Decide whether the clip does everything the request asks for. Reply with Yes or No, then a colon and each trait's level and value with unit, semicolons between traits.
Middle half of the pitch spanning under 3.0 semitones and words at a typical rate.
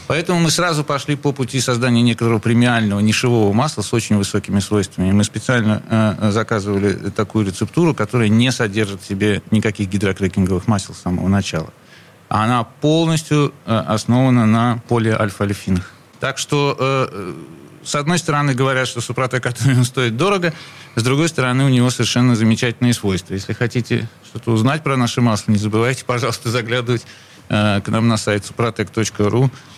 No: average, 3.5 semitones; average, 150 wpm